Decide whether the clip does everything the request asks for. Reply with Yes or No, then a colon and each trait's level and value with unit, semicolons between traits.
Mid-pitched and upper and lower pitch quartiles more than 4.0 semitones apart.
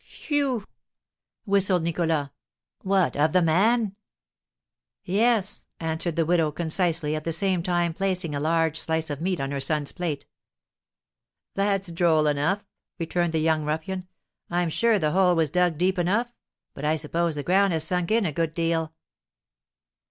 No: medium, 170 Hz; average, 3.0 semitones